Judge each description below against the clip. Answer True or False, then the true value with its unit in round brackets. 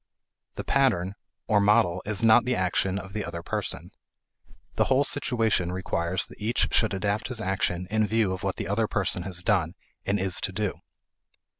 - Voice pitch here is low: True (100 Hz)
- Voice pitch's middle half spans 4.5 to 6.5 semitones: False (3.2 semitones)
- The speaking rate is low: False (180 wpm)